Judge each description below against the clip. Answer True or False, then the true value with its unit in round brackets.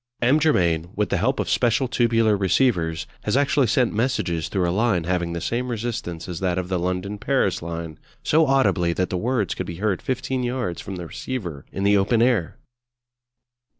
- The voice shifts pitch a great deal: True (5.9 semitones)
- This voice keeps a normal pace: True (190 wpm)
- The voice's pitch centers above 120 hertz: False (100 Hz)